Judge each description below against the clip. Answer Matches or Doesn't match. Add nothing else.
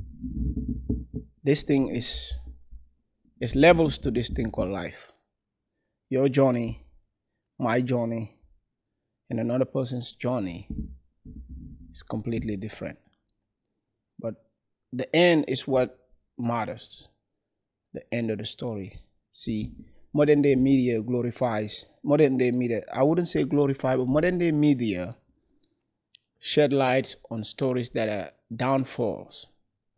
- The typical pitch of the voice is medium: Doesn't match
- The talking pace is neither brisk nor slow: Doesn't match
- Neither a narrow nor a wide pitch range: Matches